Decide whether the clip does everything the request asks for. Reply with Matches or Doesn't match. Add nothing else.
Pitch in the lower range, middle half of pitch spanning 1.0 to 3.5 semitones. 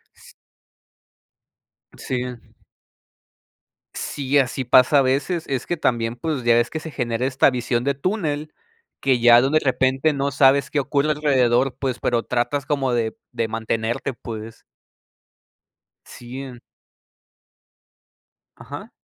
Matches